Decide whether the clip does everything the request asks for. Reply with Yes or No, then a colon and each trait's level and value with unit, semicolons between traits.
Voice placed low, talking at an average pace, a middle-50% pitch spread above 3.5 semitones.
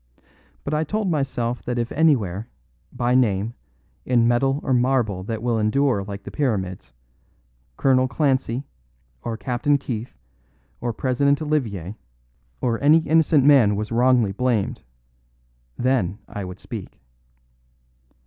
No: low, 125 Hz; slow, 125 wpm; average, 4.1 semitones